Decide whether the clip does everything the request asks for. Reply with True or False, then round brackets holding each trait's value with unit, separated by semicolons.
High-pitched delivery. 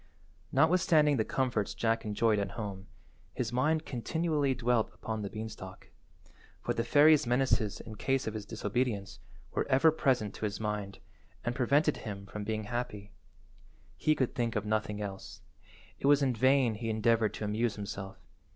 False (115 Hz)